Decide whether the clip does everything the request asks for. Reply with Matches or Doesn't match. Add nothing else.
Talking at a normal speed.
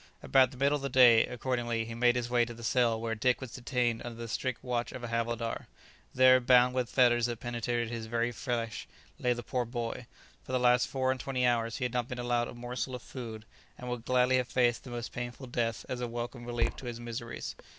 Doesn't match